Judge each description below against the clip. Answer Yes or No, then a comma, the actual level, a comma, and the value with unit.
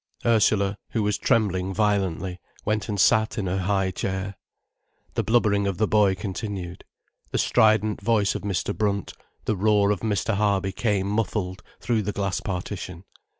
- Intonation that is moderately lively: No, narrow, 2.0 semitones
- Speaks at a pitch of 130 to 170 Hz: No, low, 100 Hz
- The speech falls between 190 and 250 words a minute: No, average, 155 wpm